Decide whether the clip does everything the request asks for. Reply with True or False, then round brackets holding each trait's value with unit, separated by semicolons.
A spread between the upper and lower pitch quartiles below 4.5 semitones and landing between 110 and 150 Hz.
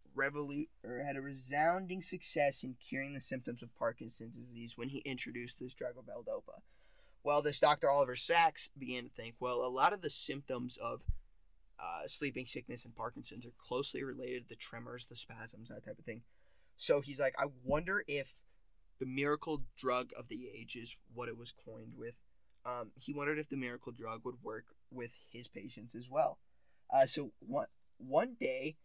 True (3.1 semitones; 130 Hz)